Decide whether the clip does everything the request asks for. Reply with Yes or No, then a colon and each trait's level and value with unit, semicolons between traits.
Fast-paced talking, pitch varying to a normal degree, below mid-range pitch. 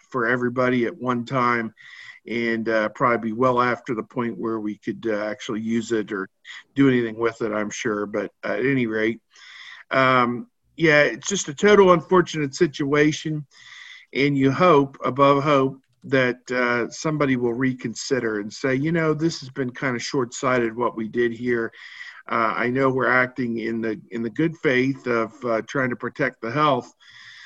No: average, 180 wpm; average, 3.2 semitones; low, 125 Hz